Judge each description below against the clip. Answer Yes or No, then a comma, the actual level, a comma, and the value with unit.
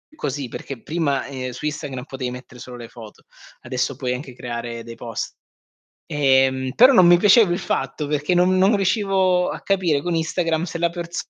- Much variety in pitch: Yes, wide, 5.7 semitones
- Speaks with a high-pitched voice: No, medium, 145 Hz